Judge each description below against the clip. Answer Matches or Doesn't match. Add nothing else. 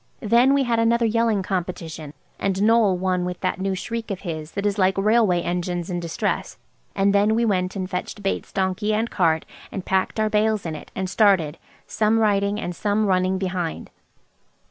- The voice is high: Matches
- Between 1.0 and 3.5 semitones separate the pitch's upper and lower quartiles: Matches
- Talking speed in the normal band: Matches